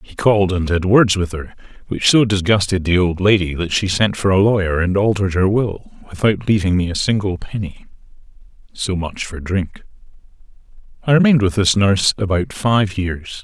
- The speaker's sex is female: No, male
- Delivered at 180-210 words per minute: Yes, average, 185 wpm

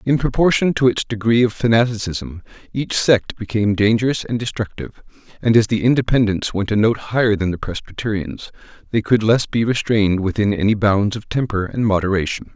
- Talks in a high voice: No, low, 110 Hz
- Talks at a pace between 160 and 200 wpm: Yes, average, 170 wpm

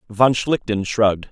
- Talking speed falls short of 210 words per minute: Yes, slow, 135 wpm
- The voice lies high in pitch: No, low, 110 Hz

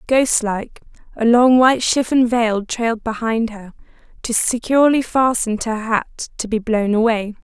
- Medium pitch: No, high, 230 Hz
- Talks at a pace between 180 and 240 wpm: No, average, 160 wpm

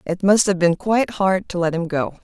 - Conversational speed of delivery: No, fast, 270 wpm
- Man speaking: No, female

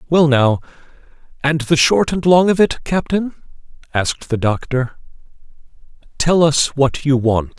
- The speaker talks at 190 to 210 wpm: No, average, 140 wpm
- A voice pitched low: No, medium, 145 Hz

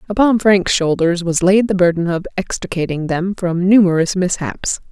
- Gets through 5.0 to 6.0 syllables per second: No, 4.8 syllables/s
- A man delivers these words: No, female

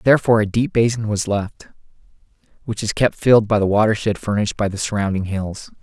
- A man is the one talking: Yes, male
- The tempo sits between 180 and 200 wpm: Yes, average, 185 wpm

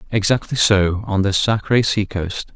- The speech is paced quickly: No, average, 165 wpm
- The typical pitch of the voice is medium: No, low, 100 Hz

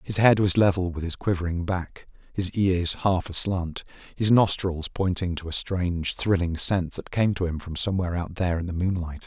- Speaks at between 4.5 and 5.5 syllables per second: Yes, 5.2 syllables/s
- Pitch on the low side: Yes, very low, 90 Hz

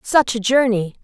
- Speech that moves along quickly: No, average, 175 wpm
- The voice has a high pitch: Yes, high, 235 Hz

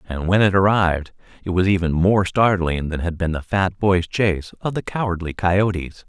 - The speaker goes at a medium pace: Yes, average, 195 wpm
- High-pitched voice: No, very low, 90 Hz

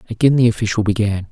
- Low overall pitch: Yes, low, 110 Hz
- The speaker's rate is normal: Yes, average, 185 wpm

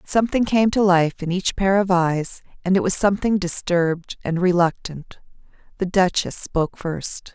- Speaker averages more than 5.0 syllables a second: No, 4.7 syllables/s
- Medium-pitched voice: Yes, medium, 180 Hz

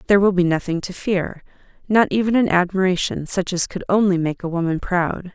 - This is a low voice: No, medium, 185 Hz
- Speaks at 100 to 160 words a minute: No, average, 200 wpm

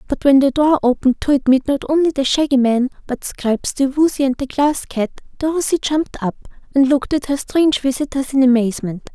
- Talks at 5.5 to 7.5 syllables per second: Yes, 5.8 syllables/s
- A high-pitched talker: Yes, very high, 270 Hz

